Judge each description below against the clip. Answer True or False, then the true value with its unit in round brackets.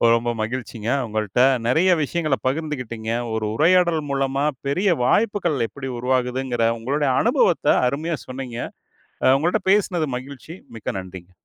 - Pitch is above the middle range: False (135 Hz)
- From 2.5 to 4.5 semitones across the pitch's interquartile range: False (5.0 semitones)